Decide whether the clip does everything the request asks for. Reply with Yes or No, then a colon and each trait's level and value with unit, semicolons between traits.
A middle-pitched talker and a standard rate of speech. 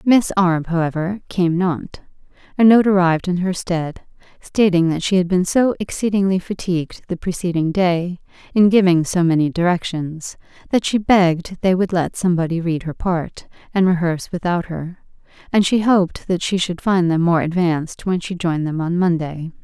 Yes: medium, 175 Hz; average, 175 wpm